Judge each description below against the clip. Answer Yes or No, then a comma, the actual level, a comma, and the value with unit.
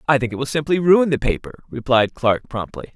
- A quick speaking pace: Yes, fast, 225 wpm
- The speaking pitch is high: No, medium, 140 Hz